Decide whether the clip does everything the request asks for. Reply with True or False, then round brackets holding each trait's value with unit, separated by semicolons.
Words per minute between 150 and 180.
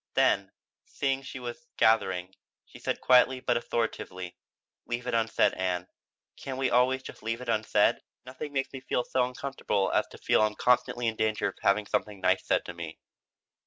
True (175 wpm)